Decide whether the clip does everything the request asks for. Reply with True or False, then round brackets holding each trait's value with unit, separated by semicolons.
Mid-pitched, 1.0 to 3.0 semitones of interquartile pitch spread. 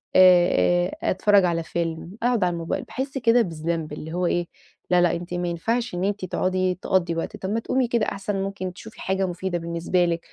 True (180 Hz; 2.6 semitones)